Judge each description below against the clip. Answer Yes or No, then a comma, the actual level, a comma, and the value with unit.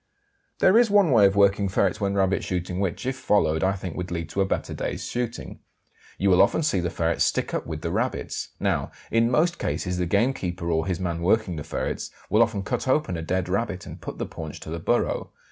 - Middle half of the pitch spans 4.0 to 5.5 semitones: Yes, average, 4.3 semitones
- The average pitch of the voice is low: Yes, very low, 95 Hz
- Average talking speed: No, fast, 230 wpm